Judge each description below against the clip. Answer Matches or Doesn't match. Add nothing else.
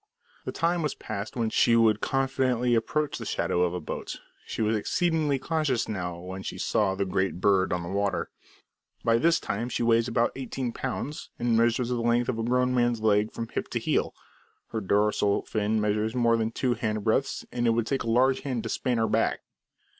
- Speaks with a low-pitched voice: Matches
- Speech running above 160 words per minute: Matches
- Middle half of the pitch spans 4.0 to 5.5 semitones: Doesn't match